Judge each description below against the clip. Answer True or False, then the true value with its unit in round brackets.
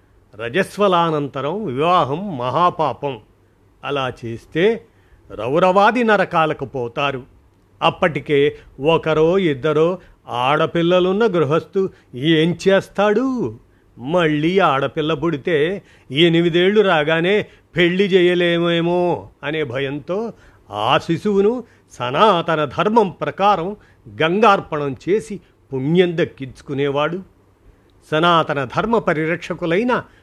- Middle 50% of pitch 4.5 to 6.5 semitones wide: True (5.2 semitones)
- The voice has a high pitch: False (160 Hz)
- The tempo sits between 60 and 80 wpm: True (70 wpm)